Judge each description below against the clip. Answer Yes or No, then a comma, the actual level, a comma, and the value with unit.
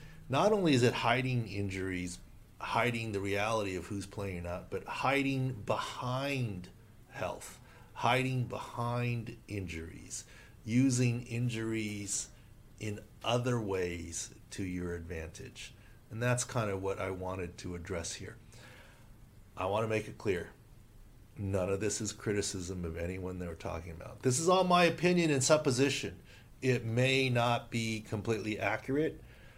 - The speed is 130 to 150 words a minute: Yes, slow, 135 wpm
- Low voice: Yes, low, 110 Hz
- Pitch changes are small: No, average, 4.0 semitones